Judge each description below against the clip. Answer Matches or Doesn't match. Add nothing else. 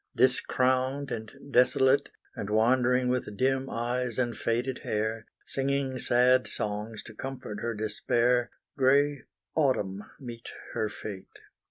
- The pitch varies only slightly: Doesn't match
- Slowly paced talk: Matches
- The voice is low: Matches